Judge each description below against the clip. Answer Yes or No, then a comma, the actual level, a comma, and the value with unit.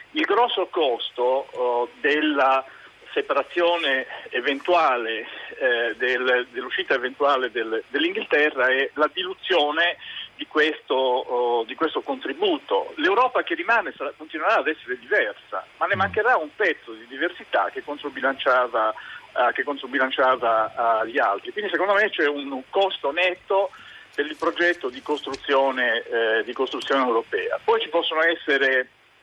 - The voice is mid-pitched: Yes, medium, 155 Hz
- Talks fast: No, average, 125 wpm